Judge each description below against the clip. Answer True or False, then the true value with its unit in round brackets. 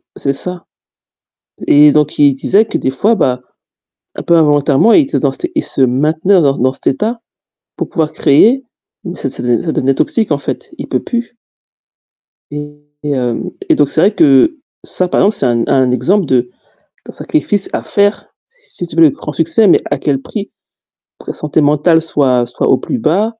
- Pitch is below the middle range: False (150 Hz)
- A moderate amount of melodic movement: False (6.4 semitones)